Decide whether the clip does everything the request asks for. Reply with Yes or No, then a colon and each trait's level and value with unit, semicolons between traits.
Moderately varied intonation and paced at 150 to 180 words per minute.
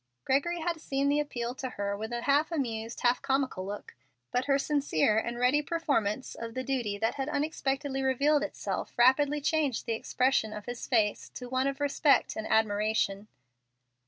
Yes: average, 4.3 semitones; average, 170 wpm